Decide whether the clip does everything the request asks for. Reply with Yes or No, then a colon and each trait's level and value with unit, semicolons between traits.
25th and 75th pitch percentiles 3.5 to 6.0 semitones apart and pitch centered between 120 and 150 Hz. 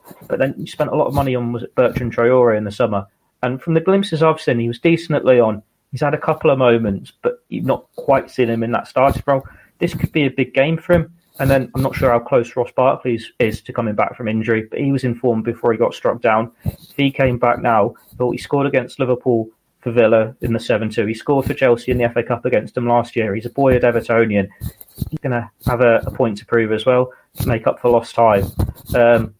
No: average, 3.1 semitones; low, 125 Hz